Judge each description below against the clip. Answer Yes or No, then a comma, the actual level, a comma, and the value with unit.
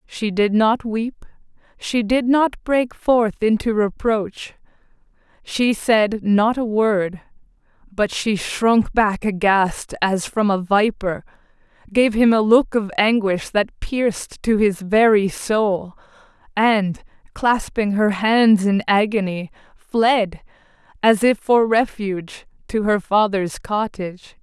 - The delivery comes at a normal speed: No, slow, 130 wpm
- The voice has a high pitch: Yes, high, 210 Hz